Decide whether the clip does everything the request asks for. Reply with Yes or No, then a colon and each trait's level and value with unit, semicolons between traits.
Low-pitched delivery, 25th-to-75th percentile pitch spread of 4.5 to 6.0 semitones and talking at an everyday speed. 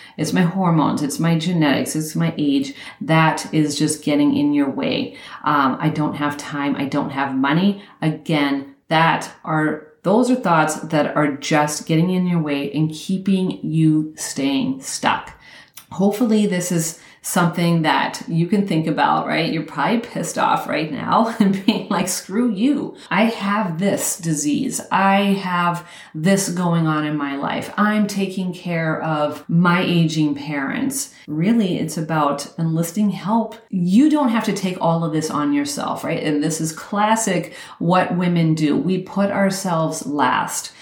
No: medium, 175 Hz; average, 4.9 semitones; average, 160 wpm